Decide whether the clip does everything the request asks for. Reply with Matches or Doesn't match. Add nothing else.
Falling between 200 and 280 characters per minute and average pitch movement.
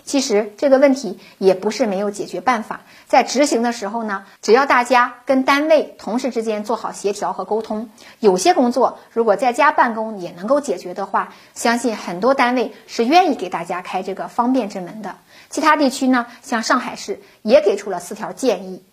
Doesn't match